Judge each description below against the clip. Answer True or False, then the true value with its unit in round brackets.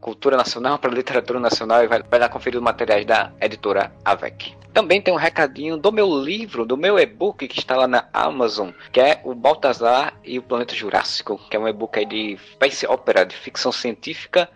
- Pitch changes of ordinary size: False (5.9 semitones)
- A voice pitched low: True (120 Hz)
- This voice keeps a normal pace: False (195 wpm)